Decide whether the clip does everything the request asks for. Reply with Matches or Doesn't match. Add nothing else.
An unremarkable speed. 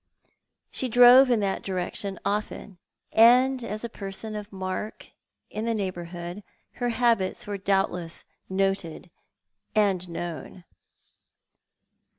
Doesn't match